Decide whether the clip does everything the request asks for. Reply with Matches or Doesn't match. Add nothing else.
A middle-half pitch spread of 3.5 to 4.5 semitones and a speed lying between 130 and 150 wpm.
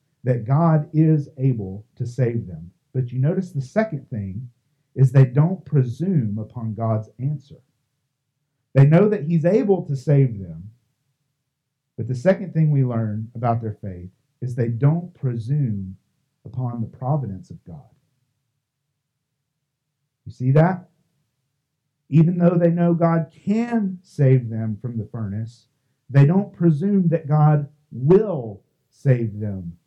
Matches